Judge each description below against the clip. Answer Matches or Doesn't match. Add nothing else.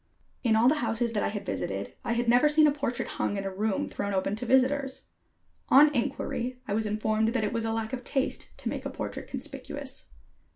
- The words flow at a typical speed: Doesn't match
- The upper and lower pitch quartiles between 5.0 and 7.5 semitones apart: Doesn't match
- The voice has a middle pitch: Doesn't match